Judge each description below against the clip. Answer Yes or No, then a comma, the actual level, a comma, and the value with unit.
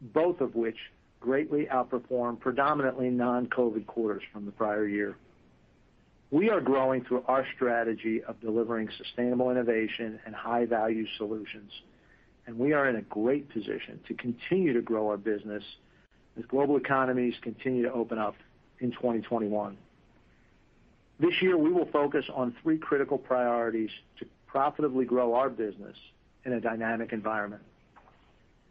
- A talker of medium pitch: No, low, 120 Hz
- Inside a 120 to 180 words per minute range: Yes, average, 140 wpm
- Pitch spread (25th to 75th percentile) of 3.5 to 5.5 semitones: No, average, 2.9 semitones